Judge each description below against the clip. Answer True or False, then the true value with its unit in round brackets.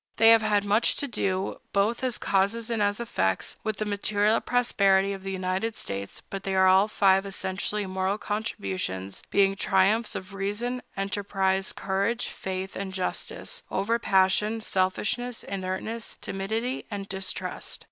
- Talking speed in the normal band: True (145 wpm)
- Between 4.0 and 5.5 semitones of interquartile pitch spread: False (2.4 semitones)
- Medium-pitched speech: False (200 Hz)